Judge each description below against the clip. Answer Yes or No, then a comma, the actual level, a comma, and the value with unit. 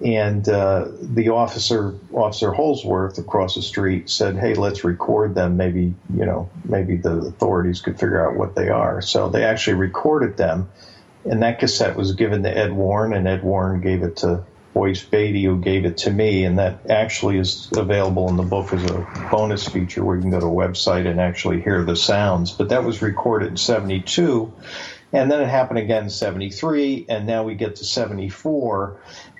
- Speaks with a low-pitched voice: Yes, very low, 95 Hz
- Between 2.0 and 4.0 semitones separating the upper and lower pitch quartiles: Yes, average, 2.9 semitones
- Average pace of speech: Yes, average, 195 wpm